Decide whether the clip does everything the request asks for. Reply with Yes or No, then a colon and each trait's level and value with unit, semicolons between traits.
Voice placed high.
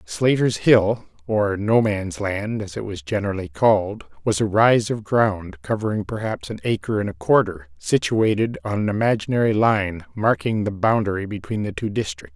No: low, 110 Hz